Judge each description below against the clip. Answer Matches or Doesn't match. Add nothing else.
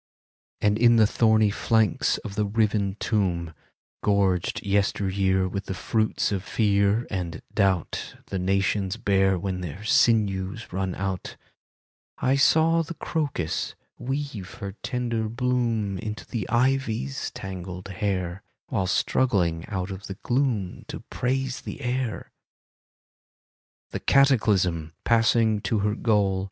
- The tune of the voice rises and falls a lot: Doesn't match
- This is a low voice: Matches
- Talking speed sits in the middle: Doesn't match